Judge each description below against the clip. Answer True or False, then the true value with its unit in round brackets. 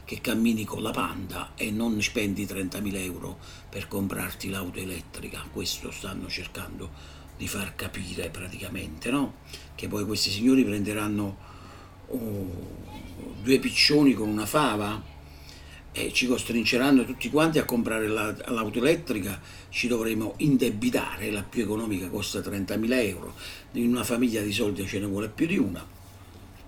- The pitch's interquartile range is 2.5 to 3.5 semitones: True (2.9 semitones)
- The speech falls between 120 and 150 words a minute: True (140 wpm)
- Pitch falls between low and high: False (100 Hz)